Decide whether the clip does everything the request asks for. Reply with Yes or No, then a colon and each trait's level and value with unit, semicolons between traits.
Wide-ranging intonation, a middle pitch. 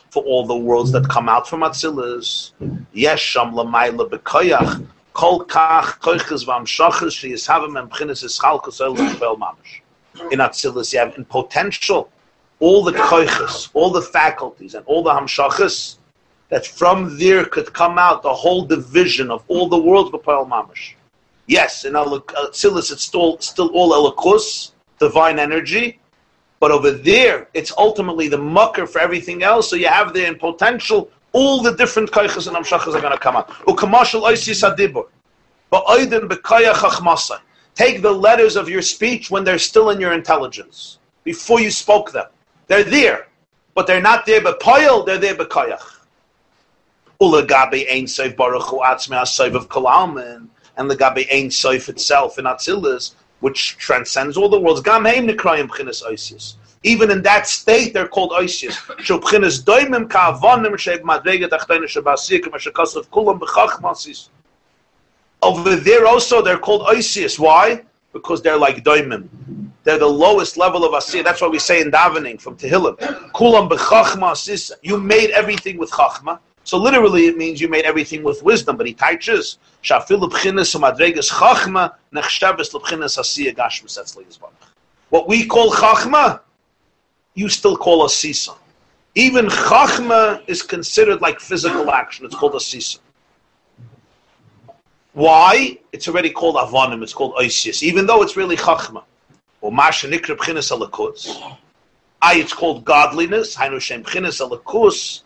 No: wide, 8.0 semitones; high, 195 Hz